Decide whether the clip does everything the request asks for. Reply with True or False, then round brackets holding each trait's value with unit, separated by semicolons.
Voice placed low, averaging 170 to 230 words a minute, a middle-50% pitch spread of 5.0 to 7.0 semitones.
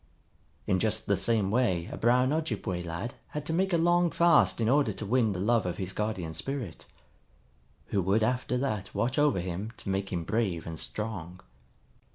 True (110 Hz; 190 wpm; 5.5 semitones)